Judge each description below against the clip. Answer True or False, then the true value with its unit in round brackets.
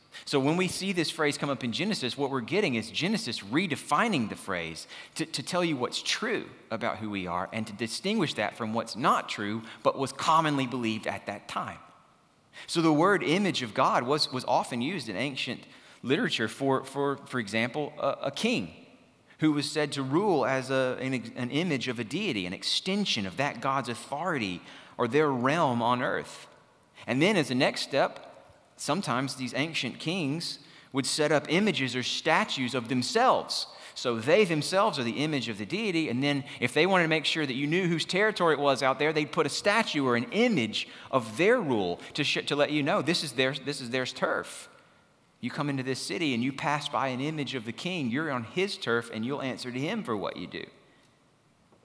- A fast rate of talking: True (210 wpm)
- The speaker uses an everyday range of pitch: True (3.8 semitones)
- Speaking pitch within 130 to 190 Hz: True (140 Hz)